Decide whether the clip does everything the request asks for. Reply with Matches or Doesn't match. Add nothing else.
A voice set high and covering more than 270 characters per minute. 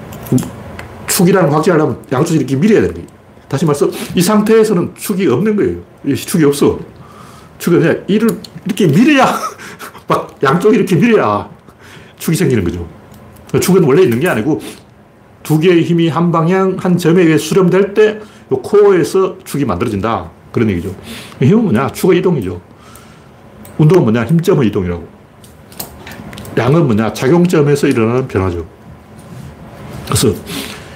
Doesn't match